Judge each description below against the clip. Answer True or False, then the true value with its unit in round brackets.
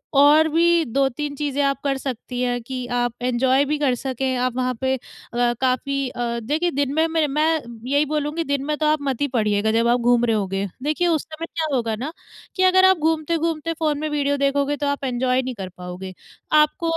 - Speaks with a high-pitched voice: True (275 Hz)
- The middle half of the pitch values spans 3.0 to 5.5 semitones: True (3.7 semitones)